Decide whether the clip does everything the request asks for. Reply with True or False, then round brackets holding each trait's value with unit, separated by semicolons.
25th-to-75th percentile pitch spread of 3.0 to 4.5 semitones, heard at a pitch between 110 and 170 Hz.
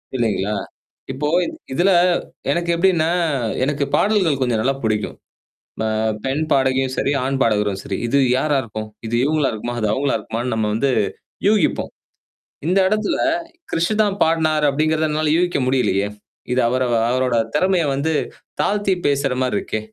False (5.0 semitones; 140 Hz)